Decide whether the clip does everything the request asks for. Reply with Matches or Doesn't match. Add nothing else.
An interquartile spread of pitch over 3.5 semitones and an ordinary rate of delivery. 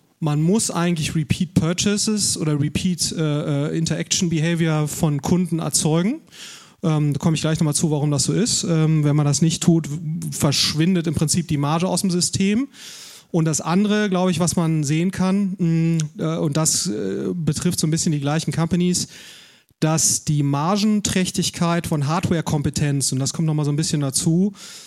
Doesn't match